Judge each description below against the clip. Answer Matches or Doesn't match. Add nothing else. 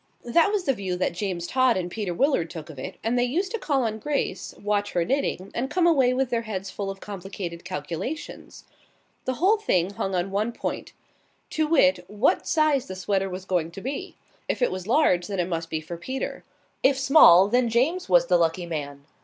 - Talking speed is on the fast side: Matches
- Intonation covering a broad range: Matches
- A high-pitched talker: Matches